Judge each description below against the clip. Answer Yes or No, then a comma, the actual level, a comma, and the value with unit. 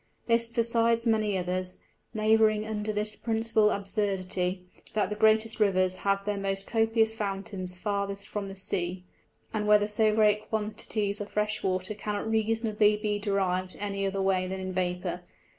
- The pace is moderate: Yes, average, 155 wpm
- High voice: Yes, high, 210 Hz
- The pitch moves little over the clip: Yes, narrow, 2.1 semitones